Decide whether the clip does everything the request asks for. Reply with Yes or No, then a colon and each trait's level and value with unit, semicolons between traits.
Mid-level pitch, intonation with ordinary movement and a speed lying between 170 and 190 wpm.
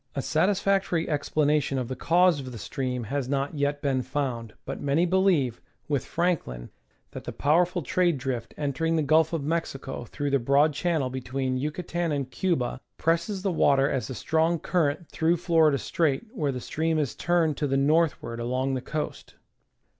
Yes: medium, 145 Hz; average, 3.9 semitones; average, 175 wpm